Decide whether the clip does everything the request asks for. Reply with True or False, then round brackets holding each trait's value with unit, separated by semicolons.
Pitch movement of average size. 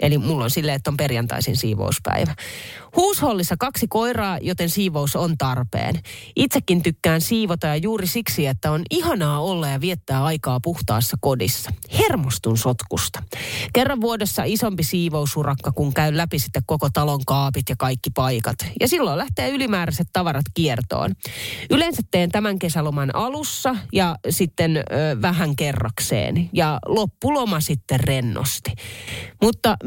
False (5.8 semitones)